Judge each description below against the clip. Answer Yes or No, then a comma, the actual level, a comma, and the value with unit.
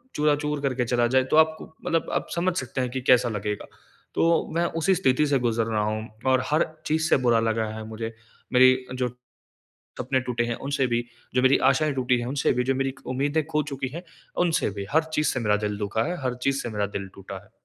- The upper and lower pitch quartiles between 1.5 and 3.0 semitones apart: No, average, 3.6 semitones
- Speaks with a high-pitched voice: No, low, 130 Hz